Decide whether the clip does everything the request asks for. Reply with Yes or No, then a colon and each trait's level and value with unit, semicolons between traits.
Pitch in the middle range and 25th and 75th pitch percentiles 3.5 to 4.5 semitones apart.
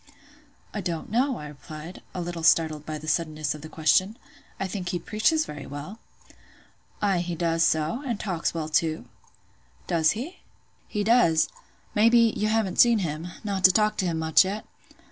No: medium, 175 Hz; average, 5.1 semitones